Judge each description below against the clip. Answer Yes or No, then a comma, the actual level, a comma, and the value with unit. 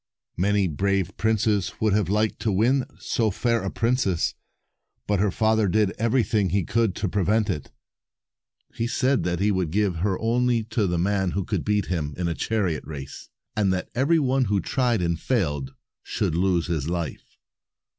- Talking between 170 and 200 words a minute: Yes, average, 180 wpm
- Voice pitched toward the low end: Yes, low, 100 Hz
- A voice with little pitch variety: No, average, 4.0 semitones